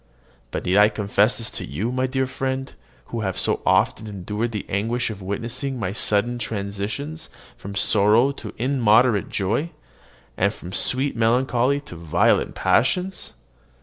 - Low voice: Yes, low, 115 Hz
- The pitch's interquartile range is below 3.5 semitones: No, average, 4.3 semitones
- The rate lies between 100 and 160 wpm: Yes, average, 150 wpm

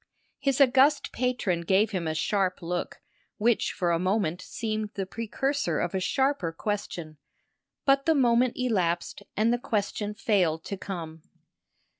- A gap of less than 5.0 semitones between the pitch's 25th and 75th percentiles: No, wide, 5.6 semitones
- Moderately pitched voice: No, high, 205 Hz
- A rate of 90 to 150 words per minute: Yes, average, 145 wpm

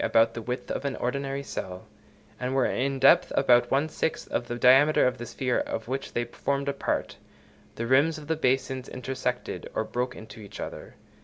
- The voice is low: Yes, low, 130 Hz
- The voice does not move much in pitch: Yes, narrow, 2.2 semitones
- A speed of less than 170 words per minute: No, fast, 205 wpm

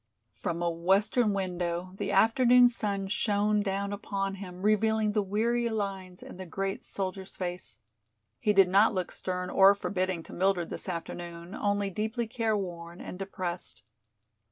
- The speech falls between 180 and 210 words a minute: No, average, 150 wpm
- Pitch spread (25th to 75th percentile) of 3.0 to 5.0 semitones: No, narrow, 2.5 semitones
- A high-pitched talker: Yes, high, 195 Hz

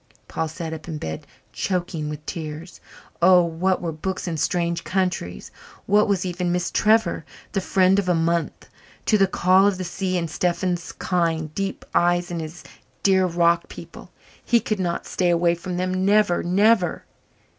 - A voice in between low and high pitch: Yes, medium, 175 Hz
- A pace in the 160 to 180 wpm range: Yes, average, 170 wpm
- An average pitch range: No, narrow, 1.9 semitones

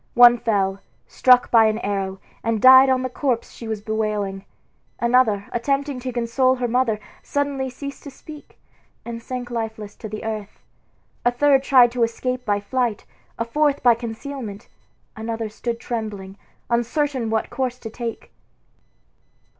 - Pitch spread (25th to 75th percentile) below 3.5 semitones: Yes, average, 2.9 semitones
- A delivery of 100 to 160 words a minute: Yes, average, 150 wpm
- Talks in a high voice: Yes, high, 235 Hz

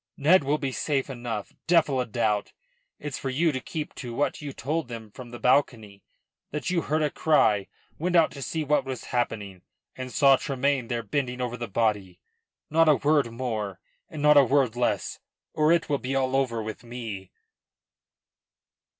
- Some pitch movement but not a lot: Yes, average, 4.1 semitones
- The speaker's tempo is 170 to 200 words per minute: Yes, average, 185 wpm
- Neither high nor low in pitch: No, low, 130 Hz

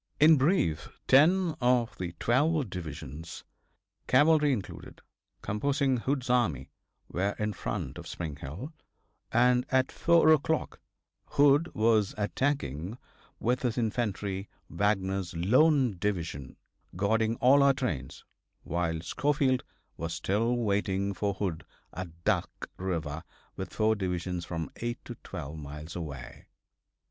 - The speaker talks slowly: Yes, slow, 120 wpm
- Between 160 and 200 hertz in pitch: No, low, 105 Hz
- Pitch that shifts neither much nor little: No, wide, 7.3 semitones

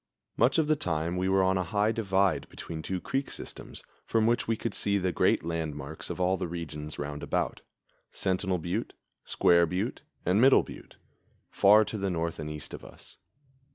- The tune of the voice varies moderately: Yes, average, 3.6 semitones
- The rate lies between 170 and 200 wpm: Yes, average, 185 wpm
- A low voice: Yes, very low, 90 Hz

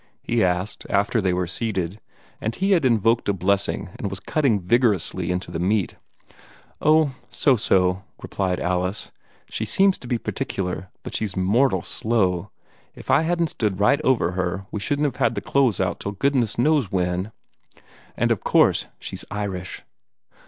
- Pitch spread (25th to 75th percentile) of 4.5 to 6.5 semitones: Yes, average, 5.1 semitones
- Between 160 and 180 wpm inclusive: Yes, average, 165 wpm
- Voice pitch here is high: No, low, 100 Hz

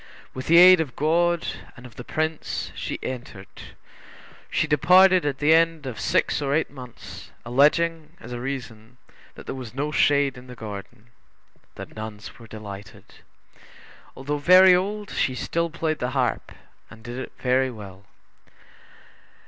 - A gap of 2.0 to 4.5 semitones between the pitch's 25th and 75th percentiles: No, average, 5.1 semitones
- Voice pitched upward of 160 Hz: No, low, 135 Hz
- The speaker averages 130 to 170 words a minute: Yes, average, 155 wpm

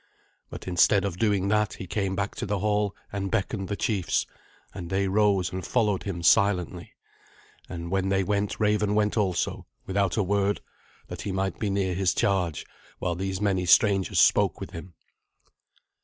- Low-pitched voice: Yes, very low, 95 Hz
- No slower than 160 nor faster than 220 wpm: Yes, average, 170 wpm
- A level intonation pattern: Yes, narrow, 1.7 semitones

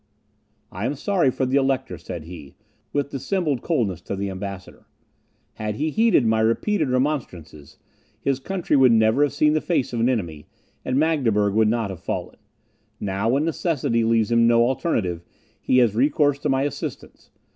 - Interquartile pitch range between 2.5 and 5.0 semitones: No, wide, 5.4 semitones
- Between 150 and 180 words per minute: Yes, average, 170 wpm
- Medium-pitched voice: No, low, 125 Hz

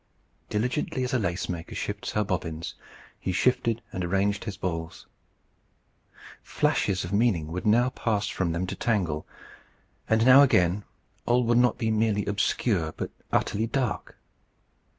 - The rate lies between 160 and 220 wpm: No, average, 145 wpm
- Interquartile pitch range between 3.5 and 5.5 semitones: Yes, average, 4.3 semitones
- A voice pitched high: No, low, 105 Hz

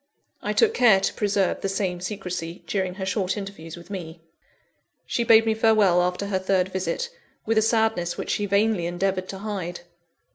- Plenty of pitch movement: No, average, 2.9 semitones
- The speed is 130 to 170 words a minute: No, average, 180 wpm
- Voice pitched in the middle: No, high, 195 Hz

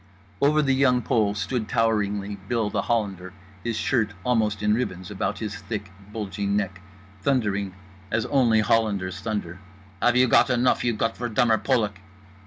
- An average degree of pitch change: Yes, average, 3.1 semitones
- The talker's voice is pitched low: Yes, low, 110 Hz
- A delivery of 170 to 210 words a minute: No, average, 150 wpm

